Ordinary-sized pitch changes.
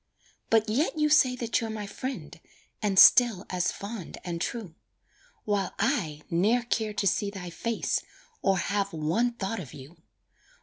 Yes: average, 4.4 semitones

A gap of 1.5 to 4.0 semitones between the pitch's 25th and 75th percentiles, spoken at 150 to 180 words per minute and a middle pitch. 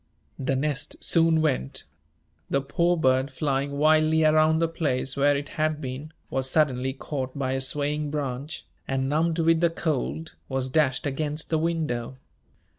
Yes: average, 2.9 semitones; average, 155 wpm; medium, 145 Hz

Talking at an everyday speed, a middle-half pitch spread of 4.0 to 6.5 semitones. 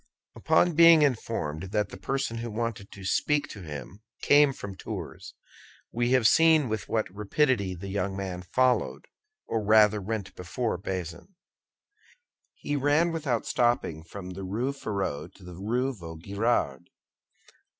Yes: average, 145 wpm; wide, 5.4 semitones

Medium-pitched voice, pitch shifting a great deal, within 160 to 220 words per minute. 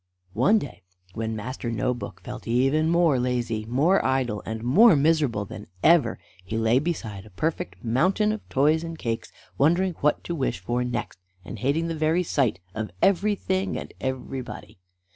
No: low, 130 Hz; wide, 6.3 semitones; average, 165 wpm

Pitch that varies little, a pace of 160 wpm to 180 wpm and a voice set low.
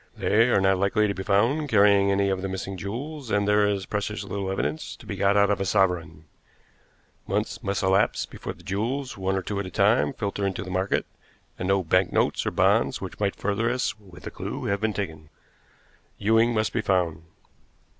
No: narrow, 1.8 semitones; fast, 205 wpm; low, 100 Hz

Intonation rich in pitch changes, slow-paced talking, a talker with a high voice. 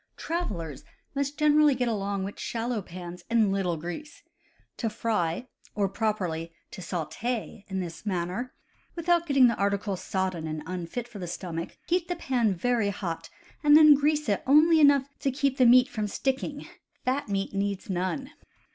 No: wide, 6.9 semitones; average, 165 wpm; high, 215 Hz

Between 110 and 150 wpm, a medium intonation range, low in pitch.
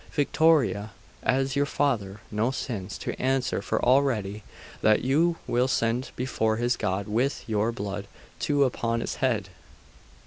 Yes: average, 140 wpm; average, 4.1 semitones; low, 120 Hz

